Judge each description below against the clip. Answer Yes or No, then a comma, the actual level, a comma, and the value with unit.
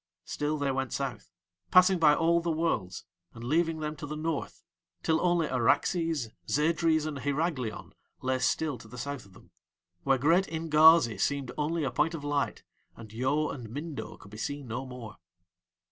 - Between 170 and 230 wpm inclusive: Yes, average, 175 wpm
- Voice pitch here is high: No, medium, 145 Hz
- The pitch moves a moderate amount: Yes, average, 4.0 semitones